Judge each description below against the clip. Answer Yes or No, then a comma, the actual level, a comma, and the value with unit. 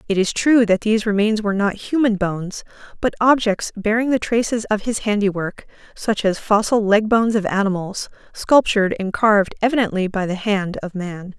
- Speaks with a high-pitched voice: Yes, high, 210 Hz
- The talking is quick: No, average, 180 wpm